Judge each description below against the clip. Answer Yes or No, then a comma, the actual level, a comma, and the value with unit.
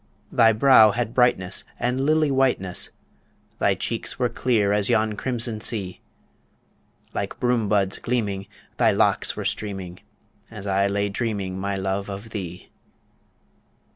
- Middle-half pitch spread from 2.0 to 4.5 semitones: Yes, average, 3.7 semitones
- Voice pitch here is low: Yes, low, 105 Hz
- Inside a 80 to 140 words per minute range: Yes, slow, 135 wpm